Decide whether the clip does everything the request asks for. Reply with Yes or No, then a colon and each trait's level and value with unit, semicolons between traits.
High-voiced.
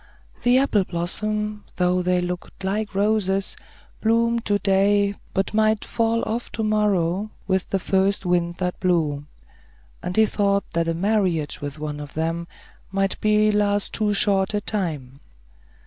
Yes: high, 195 Hz